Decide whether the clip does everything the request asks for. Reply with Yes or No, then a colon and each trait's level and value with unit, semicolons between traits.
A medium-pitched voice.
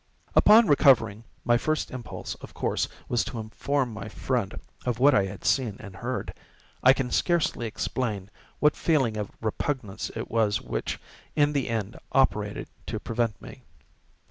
No: low, 120 Hz